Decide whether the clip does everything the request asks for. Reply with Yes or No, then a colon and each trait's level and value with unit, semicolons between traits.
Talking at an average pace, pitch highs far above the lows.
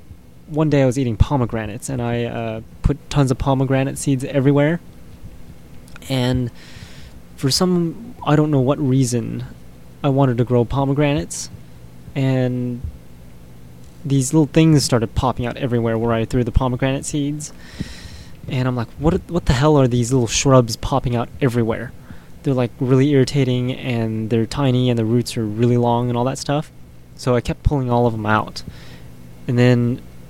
No: average, 165 wpm; average, 3.7 semitones